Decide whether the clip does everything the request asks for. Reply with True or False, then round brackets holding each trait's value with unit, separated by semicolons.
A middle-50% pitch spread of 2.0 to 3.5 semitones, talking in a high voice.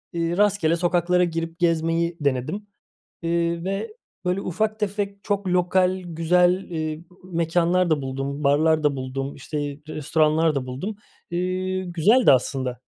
False (3.0 semitones; 170 Hz)